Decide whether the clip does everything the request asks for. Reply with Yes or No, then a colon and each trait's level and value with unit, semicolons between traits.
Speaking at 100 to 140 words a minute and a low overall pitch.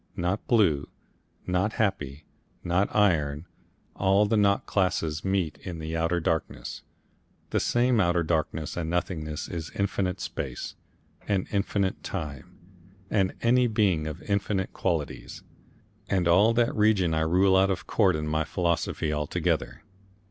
Yes: slow, 135 wpm; very low, 90 Hz